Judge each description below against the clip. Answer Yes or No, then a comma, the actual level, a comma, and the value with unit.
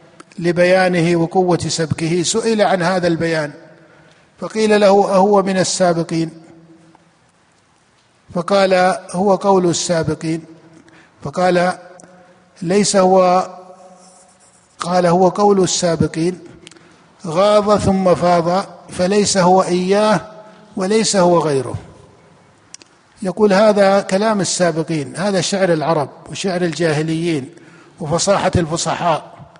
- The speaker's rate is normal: Yes, average, 85 wpm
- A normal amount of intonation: No, narrow, 2.2 semitones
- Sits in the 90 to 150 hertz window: No, medium, 180 Hz